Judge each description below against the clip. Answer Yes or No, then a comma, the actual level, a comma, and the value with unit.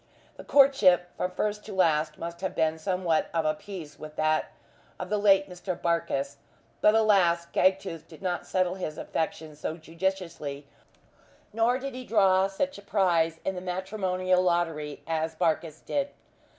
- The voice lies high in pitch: No, medium, 180 Hz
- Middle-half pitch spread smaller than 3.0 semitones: No, average, 3.3 semitones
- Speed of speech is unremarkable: Yes, average, 160 wpm